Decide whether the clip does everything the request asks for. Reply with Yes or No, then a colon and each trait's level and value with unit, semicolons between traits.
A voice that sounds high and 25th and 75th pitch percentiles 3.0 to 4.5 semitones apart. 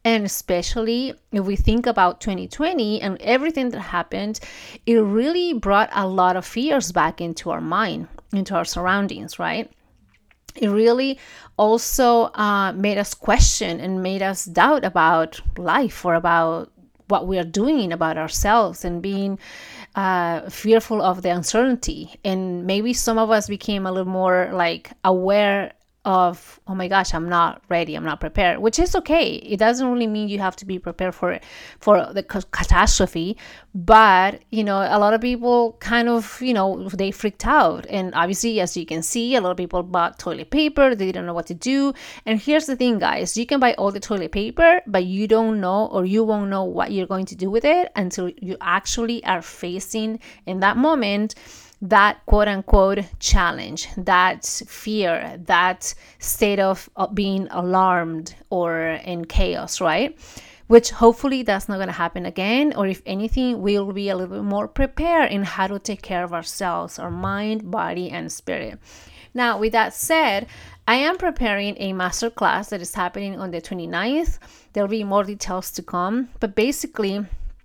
Yes: high, 200 Hz; average, 3.8 semitones